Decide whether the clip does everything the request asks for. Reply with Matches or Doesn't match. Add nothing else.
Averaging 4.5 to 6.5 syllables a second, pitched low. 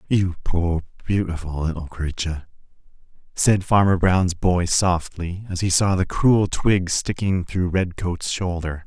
Doesn't match